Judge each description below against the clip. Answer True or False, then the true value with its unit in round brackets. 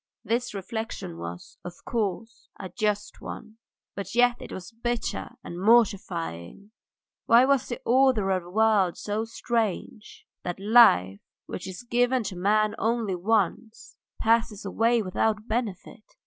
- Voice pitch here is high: True (215 Hz)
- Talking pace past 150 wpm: False (135 wpm)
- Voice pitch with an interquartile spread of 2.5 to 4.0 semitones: True (3.6 semitones)